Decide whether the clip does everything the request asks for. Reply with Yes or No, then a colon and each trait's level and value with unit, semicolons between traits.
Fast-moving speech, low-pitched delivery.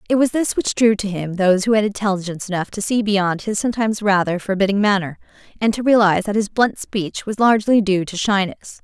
No: fast, 215 wpm; high, 205 Hz